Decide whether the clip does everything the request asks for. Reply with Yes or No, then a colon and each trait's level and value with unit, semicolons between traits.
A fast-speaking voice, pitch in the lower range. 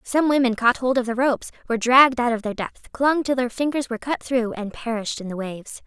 No: fast, 255 wpm; high, 245 Hz